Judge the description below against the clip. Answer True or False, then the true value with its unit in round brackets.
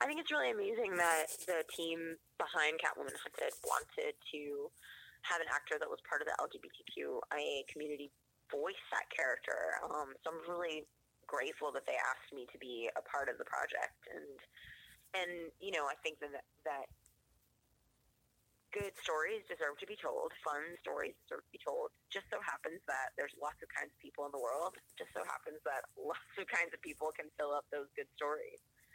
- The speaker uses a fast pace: False (185 wpm)